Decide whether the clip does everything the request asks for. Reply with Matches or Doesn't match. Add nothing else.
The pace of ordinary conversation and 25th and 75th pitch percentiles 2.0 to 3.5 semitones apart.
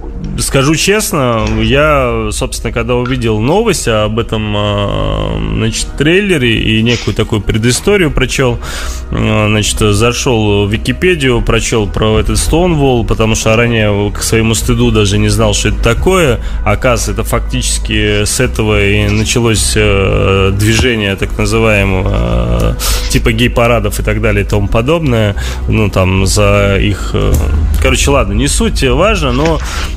Matches